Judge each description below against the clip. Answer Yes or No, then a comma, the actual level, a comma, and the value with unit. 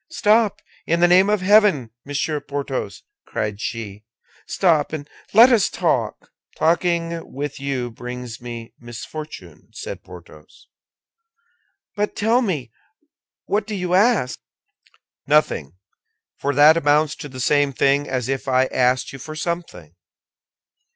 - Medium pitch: Yes, medium, 145 Hz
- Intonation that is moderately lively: No, wide, 6.0 semitones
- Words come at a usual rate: No, slow, 130 wpm